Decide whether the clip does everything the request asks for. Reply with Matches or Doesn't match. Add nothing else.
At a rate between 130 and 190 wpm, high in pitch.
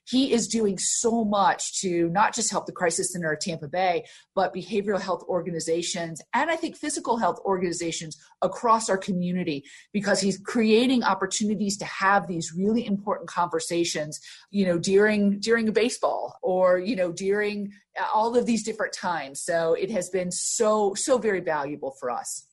Matches